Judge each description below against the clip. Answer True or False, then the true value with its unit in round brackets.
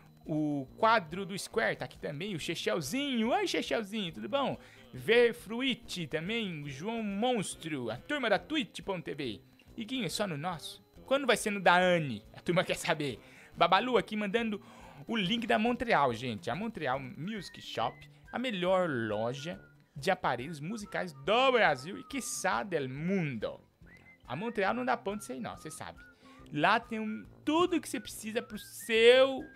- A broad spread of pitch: True (7.0 semitones)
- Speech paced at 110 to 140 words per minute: False (165 wpm)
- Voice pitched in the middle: False (195 Hz)